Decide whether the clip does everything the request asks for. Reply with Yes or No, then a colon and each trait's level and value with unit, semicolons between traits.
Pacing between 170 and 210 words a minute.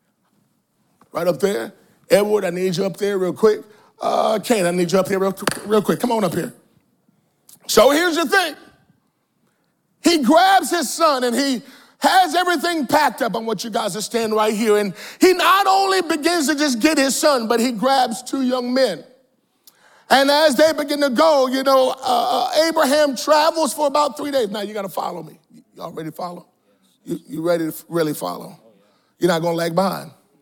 Yes: average, 195 wpm